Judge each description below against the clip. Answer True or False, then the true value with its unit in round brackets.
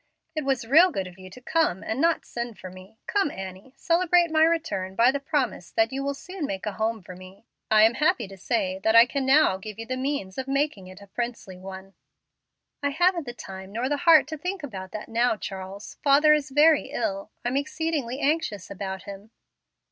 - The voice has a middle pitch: False (240 Hz)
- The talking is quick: True (215 wpm)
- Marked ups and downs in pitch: True (7.2 semitones)